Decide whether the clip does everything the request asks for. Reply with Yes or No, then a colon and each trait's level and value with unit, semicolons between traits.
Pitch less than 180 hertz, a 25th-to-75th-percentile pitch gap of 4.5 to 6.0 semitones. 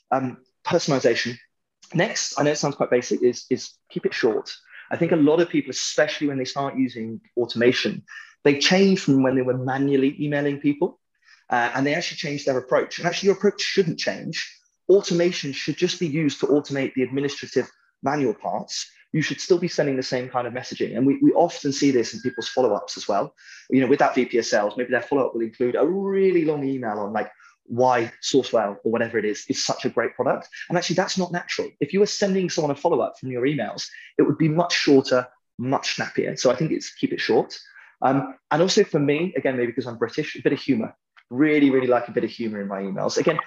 Yes: medium, 140 Hz; average, 5.2 semitones